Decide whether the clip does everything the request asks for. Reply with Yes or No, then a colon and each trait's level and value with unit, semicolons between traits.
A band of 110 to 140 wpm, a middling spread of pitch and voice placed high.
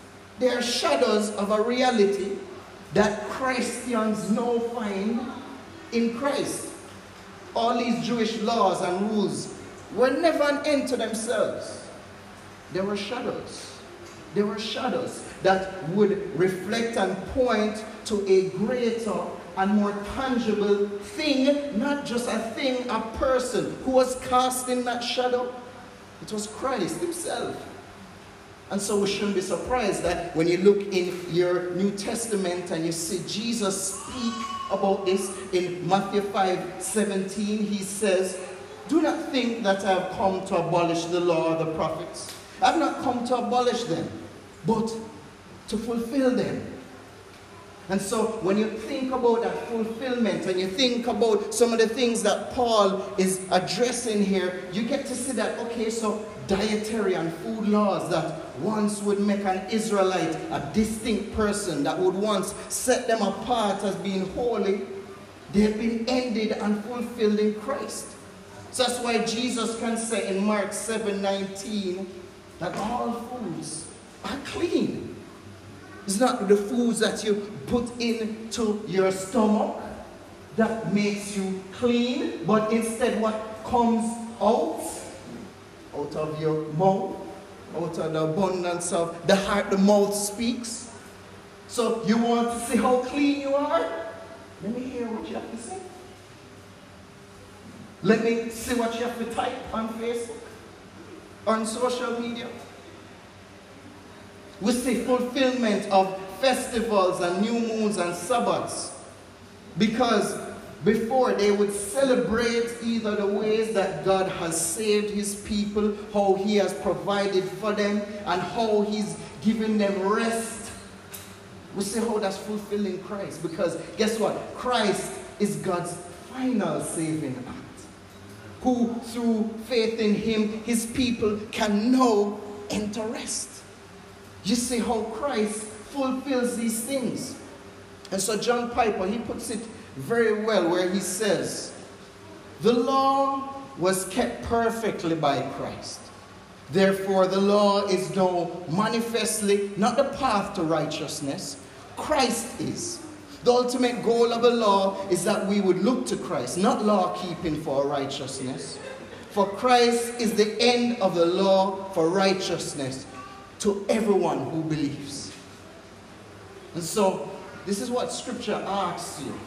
Yes: slow, 135 wpm; average, 3.8 semitones; high, 210 Hz